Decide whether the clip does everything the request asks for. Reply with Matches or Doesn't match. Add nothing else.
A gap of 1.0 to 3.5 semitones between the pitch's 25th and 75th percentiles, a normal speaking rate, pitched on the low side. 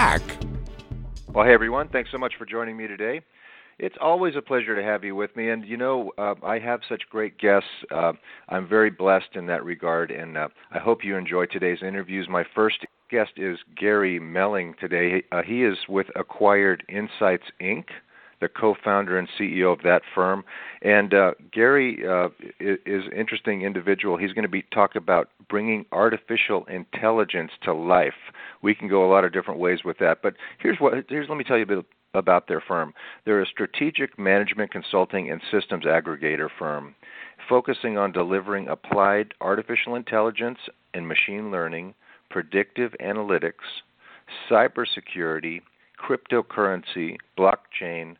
Matches